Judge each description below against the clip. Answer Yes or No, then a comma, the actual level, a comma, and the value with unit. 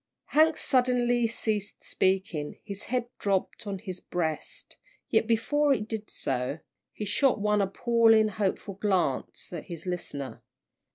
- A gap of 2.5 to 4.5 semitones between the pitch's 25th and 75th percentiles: Yes, average, 3.9 semitones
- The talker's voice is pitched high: Yes, high, 210 Hz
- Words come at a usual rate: No, slow, 130 wpm